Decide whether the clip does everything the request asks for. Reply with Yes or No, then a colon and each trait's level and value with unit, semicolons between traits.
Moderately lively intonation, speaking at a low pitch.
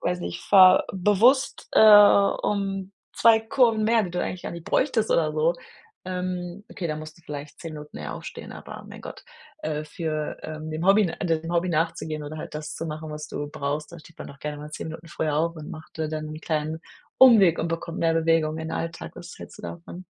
No: average, 3.2 semitones; medium, 165 Hz